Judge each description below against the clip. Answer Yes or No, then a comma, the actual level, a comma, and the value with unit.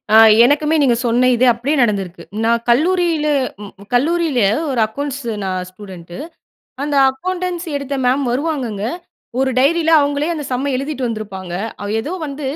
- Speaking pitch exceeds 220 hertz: Yes, very high, 270 Hz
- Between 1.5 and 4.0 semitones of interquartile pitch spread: No, average, 4.7 semitones